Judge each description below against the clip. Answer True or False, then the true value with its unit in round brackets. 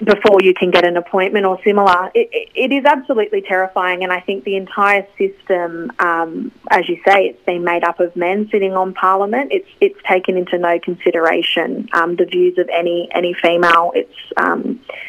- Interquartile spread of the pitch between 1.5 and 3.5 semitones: True (2.6 semitones)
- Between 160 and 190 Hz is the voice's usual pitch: True (185 Hz)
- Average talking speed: True (190 wpm)